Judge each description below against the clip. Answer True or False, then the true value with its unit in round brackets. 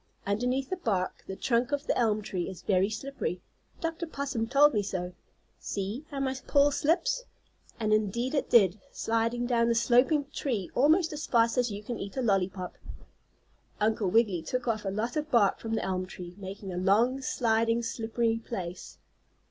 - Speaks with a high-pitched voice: True (230 Hz)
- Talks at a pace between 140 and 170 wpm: False (180 wpm)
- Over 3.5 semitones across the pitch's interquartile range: True (4.8 semitones)